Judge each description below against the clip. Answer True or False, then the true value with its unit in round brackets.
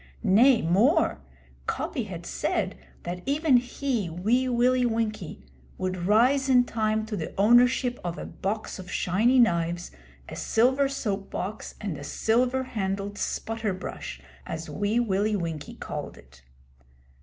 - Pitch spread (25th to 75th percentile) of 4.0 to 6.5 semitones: True (4.9 semitones)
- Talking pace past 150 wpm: False (140 wpm)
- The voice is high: True (215 Hz)